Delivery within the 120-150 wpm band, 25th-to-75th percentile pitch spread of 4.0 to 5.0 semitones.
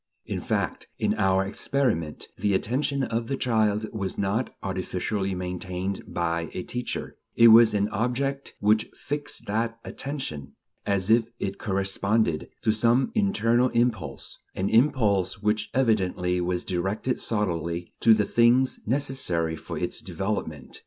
Yes: average, 140 wpm; average, 4.3 semitones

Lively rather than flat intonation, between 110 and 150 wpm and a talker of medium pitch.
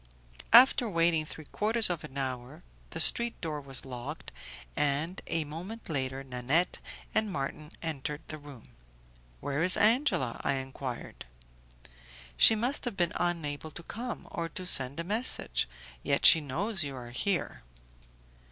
Yes: wide, 5.8 semitones; average, 145 wpm; medium, 160 Hz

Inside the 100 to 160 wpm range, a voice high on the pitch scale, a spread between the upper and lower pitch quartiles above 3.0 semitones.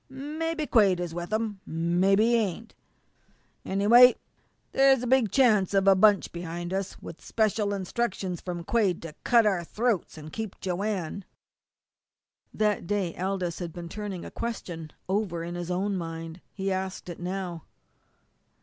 Yes: average, 155 wpm; high, 195 Hz; average, 3.8 semitones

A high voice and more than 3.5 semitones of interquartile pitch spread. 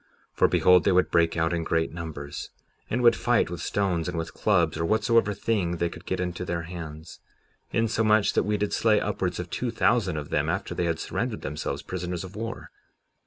No: very low, 90 Hz; average, 4.1 semitones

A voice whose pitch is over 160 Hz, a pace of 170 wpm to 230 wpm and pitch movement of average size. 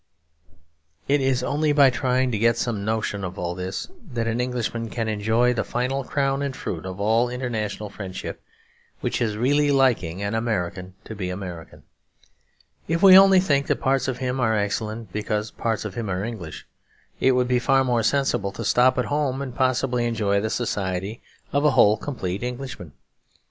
No: low, 115 Hz; average, 180 wpm; average, 4.2 semitones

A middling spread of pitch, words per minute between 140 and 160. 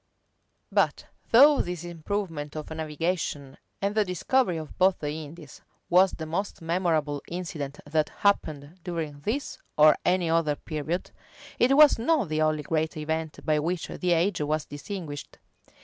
Yes: average, 3.3 semitones; average, 150 wpm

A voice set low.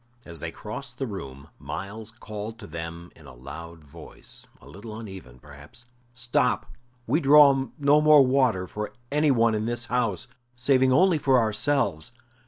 Yes: low, 110 Hz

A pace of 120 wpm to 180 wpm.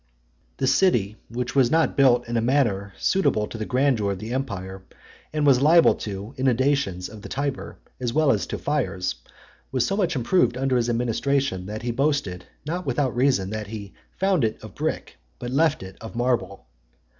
No: average, 190 wpm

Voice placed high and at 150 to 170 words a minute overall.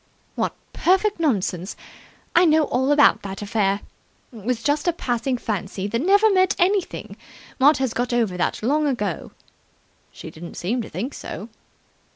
Yes: high, 245 Hz; average, 160 wpm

